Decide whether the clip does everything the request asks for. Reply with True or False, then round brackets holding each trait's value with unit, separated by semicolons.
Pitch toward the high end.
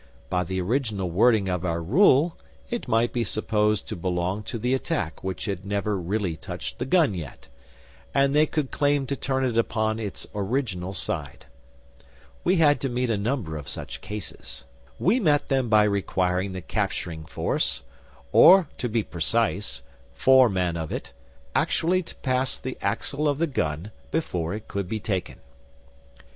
False (110 Hz)